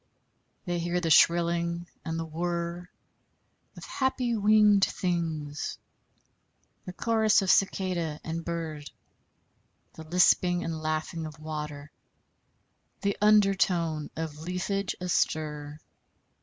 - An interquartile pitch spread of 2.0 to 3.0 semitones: Yes, average, 2.7 semitones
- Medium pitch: Yes, medium, 170 Hz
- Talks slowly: Yes, slow, 105 wpm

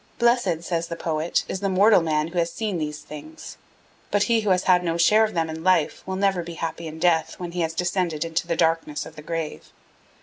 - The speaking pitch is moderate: Yes, medium, 170 Hz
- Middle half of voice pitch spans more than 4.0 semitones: No, narrow, 2.5 semitones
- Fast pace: Yes, fast, 235 wpm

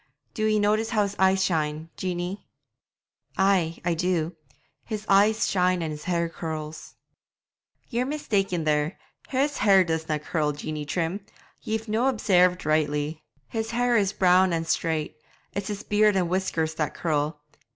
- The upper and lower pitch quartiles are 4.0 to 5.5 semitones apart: Yes, average, 4.6 semitones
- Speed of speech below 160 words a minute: Yes, average, 150 wpm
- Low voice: No, medium, 180 Hz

